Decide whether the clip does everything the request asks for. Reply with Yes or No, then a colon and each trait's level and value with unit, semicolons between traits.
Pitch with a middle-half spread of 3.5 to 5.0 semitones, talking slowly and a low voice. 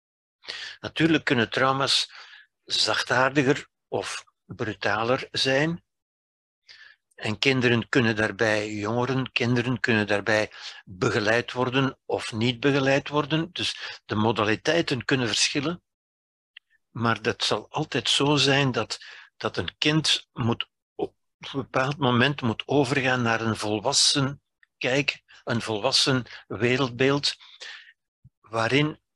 Yes: average, 3.8 semitones; slow, 105 wpm; low, 130 Hz